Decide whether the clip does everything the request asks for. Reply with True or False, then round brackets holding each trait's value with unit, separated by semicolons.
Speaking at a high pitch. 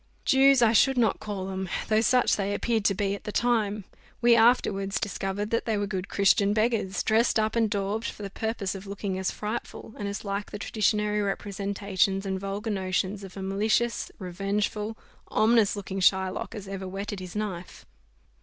True (205 Hz)